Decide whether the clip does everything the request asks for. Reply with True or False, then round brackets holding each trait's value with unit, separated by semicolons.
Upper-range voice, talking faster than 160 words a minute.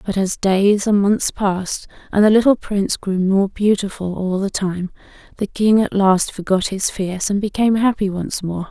True (200 Hz; 195 wpm)